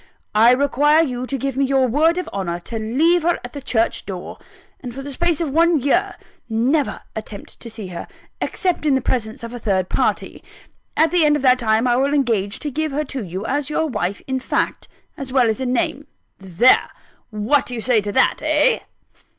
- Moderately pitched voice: No, very high, 260 Hz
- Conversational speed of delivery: No, fast, 215 wpm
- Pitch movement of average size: Yes, average, 4.8 semitones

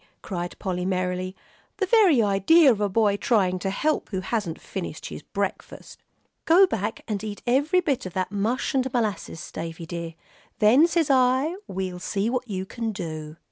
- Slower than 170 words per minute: No, average, 175 wpm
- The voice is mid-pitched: No, high, 205 Hz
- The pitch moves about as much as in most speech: No, wide, 5.8 semitones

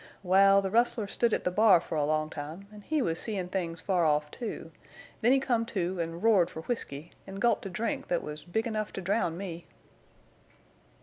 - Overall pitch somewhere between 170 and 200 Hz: Yes, high, 190 Hz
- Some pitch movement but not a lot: Yes, average, 4.9 semitones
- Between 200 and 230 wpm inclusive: Yes, fast, 205 wpm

